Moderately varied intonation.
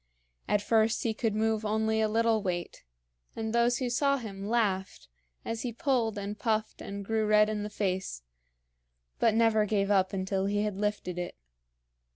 No: narrow, 2.0 semitones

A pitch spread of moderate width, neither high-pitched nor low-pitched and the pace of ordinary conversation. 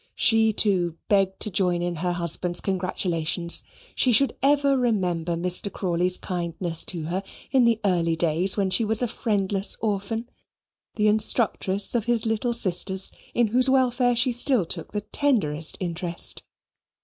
No: average, 4.7 semitones; high, 195 Hz; average, 150 wpm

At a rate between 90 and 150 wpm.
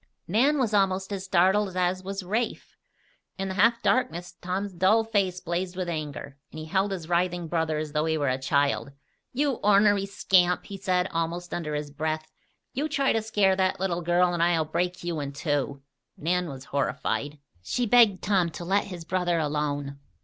No: average, 185 wpm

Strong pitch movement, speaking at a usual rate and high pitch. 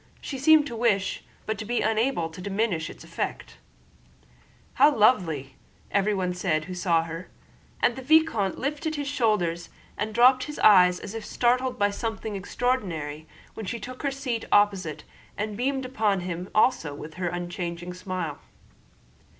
Yes: wide, 5.7 semitones; average, 155 wpm; high, 205 Hz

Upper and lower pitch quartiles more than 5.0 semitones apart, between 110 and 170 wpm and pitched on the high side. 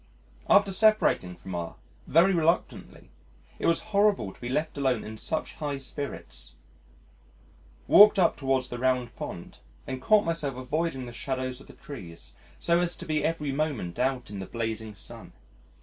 No: wide, 5.6 semitones; average, 165 wpm; low, 135 Hz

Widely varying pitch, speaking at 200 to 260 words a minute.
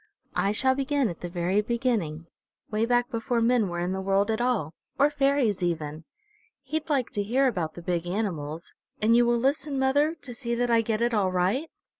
Yes: wide, 6.3 semitones; fast, 205 wpm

